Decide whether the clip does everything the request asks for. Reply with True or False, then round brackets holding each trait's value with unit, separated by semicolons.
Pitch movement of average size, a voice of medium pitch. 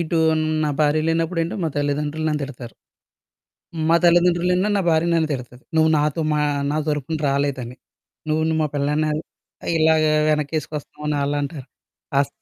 False (2.1 semitones; 155 Hz)